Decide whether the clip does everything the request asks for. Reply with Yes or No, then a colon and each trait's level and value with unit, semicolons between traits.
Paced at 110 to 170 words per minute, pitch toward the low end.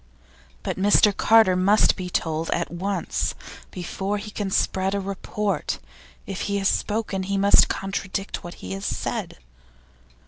No: average, 145 wpm; high, 195 Hz